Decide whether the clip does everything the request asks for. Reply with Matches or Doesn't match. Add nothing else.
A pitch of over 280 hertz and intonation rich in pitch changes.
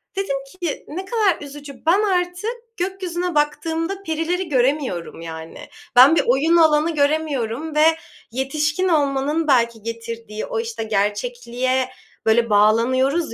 Matches